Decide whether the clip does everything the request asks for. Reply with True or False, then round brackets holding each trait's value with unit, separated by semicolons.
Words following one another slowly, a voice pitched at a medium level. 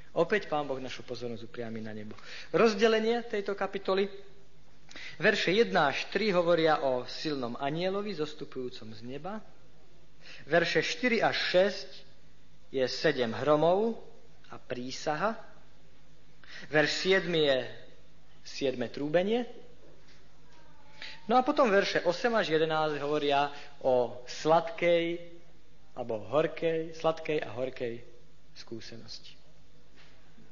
True (100 wpm; 155 Hz)